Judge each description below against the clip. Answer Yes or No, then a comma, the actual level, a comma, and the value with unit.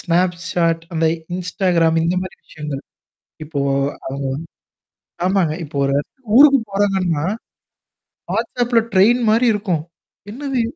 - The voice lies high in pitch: No, medium, 180 Hz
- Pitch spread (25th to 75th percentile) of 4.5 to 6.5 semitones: Yes, average, 4.8 semitones